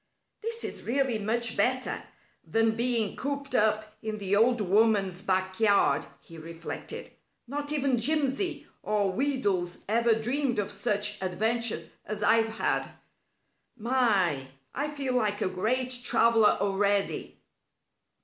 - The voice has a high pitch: Yes, high, 225 Hz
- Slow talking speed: Yes, slow, 120 wpm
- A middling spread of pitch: Yes, average, 4.0 semitones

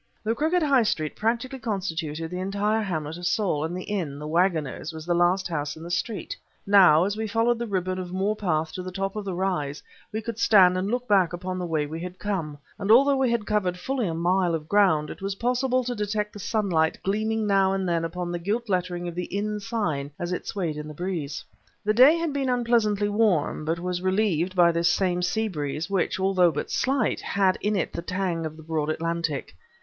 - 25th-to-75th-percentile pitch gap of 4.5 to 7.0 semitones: No, average, 4.0 semitones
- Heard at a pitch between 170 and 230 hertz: Yes, medium, 185 Hz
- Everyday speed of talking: No, fast, 225 wpm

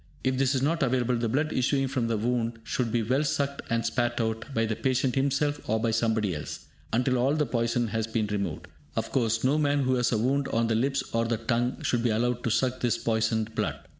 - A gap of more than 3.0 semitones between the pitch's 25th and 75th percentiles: No, average, 2.7 semitones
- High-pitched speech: No, low, 120 Hz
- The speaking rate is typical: No, fast, 235 wpm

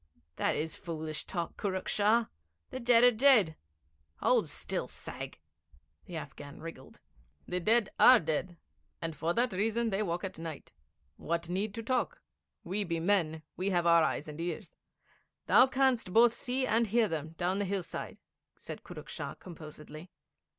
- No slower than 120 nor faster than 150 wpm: No, average, 160 wpm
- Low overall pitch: No, medium, 185 Hz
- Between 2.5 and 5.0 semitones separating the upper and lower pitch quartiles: No, wide, 5.6 semitones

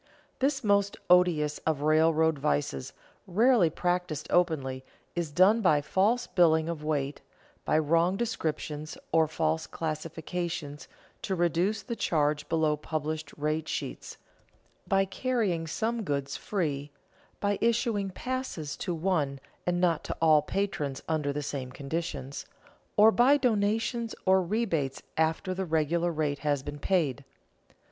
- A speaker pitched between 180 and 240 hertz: No, medium, 165 Hz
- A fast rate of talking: No, slow, 135 wpm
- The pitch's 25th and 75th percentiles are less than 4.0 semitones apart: No, average, 4.3 semitones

